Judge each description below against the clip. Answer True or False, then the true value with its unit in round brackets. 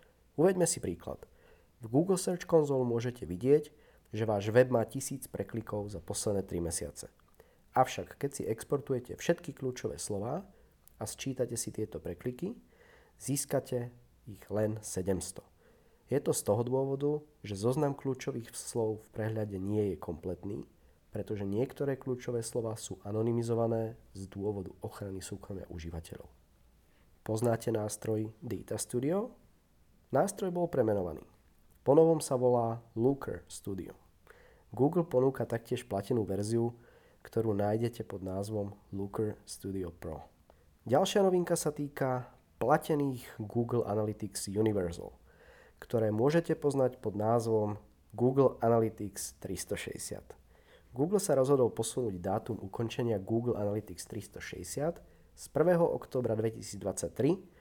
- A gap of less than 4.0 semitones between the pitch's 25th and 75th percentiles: False (4.6 semitones)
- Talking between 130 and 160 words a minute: False (120 wpm)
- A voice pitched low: True (115 Hz)